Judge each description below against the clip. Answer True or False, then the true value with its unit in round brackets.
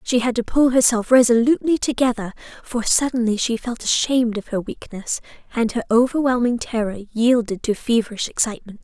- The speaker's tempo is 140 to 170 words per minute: True (155 wpm)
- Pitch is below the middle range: False (235 Hz)